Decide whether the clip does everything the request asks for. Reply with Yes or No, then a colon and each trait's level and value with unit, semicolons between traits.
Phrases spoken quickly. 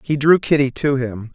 Yes: fast, 225 wpm